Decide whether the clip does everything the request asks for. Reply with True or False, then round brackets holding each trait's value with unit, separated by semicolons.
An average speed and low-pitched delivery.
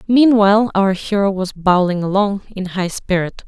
False (155 wpm; 195 Hz)